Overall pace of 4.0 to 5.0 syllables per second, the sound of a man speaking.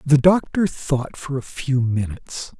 Yes: 4.1 syllables/s; male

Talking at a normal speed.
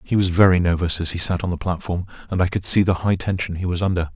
No: fast, 290 wpm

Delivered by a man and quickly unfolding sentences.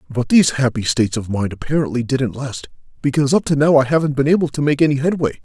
Yes: male; fast, 230 wpm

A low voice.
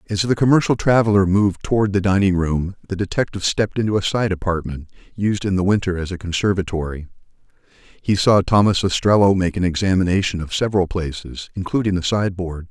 Yes: very low, 95 Hz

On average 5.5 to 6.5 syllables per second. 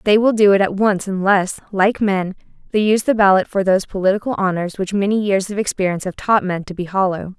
Yes: 6.0 syllables/s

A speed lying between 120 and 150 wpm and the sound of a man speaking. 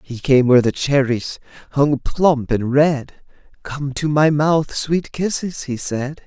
No: average, 165 wpm; male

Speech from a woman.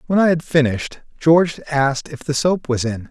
No: male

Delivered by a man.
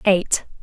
No: female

